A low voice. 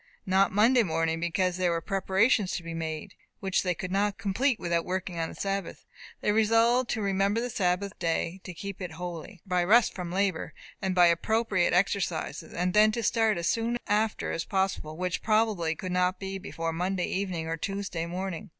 No: high, 190 Hz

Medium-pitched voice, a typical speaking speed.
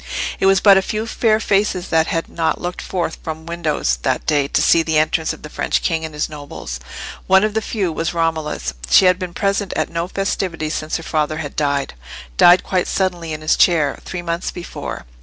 No: medium, 165 Hz; fast, 210 wpm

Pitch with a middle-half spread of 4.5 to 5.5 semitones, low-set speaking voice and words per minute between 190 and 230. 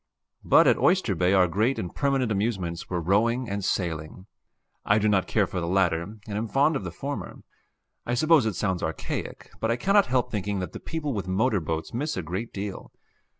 Yes: average, 4.9 semitones; low, 100 Hz; fast, 205 wpm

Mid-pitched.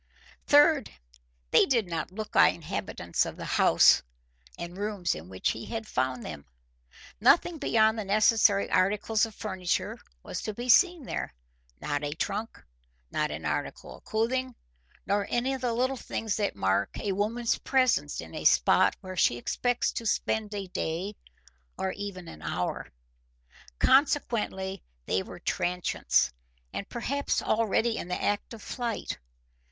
No: high, 210 Hz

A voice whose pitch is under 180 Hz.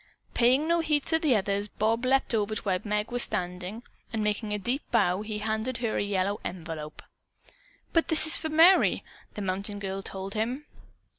No: high, 215 Hz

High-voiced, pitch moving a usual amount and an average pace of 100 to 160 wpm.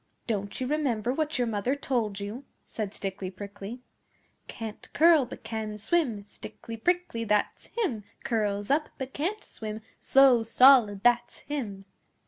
Yes: high, 230 Hz; average, 4.6 semitones; average, 140 wpm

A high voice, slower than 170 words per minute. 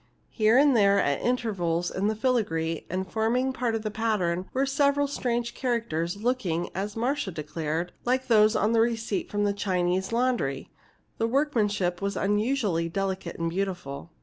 Yes: high, 205 Hz; average, 160 wpm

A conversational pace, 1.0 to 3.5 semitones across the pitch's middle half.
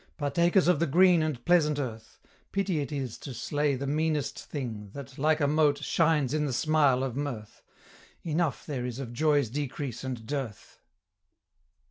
Yes: average, 165 wpm; average, 3.2 semitones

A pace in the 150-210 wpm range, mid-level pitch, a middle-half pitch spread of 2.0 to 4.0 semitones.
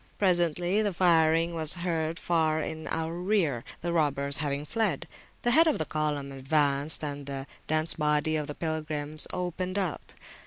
Yes: average, 155 wpm; medium, 160 Hz; average, 2.8 semitones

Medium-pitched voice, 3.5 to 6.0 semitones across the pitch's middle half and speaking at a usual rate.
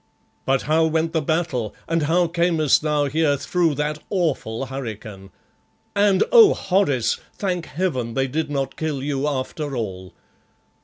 Yes: medium, 150 Hz; average, 3.8 semitones; average, 145 wpm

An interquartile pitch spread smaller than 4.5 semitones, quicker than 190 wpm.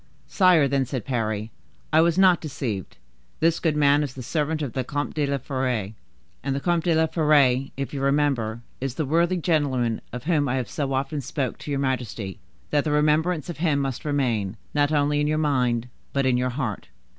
Yes: average, 3.4 semitones; fast, 205 wpm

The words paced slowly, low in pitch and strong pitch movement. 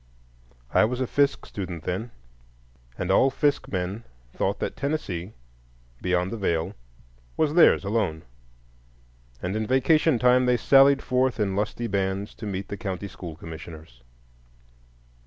Yes: slow, 130 wpm; low, 100 Hz; wide, 6.9 semitones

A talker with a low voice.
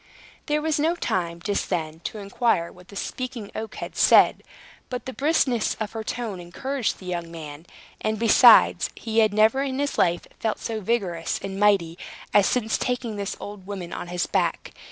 No: high, 210 Hz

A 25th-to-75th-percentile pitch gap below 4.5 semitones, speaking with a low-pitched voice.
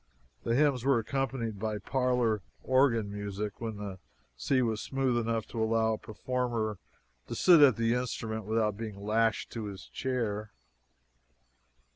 Yes: average, 2.9 semitones; low, 115 Hz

